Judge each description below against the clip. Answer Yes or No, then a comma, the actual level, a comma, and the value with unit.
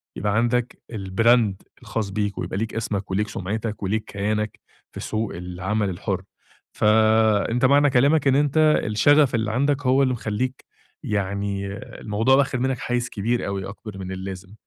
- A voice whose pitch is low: Yes, low, 110 Hz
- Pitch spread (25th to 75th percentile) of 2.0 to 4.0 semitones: Yes, average, 3.6 semitones